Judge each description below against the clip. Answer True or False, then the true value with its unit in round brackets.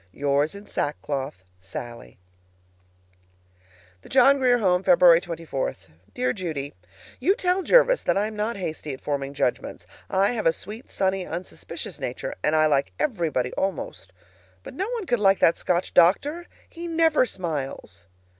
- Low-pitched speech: False (180 Hz)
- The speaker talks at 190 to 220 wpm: False (150 wpm)